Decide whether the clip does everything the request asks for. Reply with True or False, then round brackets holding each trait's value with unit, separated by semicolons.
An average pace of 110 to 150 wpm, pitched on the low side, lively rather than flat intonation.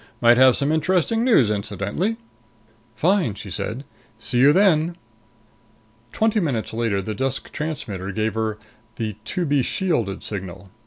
True (145 wpm; 125 Hz; 7.7 semitones)